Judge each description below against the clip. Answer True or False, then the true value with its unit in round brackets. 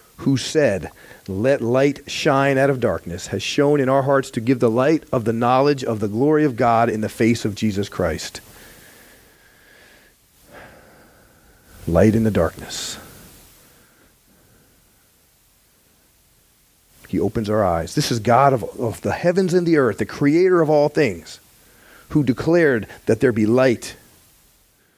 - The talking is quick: False (145 wpm)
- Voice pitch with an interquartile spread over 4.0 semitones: True (4.4 semitones)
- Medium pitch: False (130 Hz)